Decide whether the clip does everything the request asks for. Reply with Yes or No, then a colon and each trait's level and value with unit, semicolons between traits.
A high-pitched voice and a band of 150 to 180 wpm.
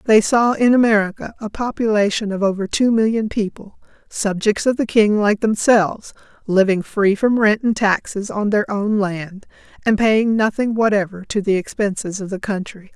Yes: high, 210 Hz; average, 170 wpm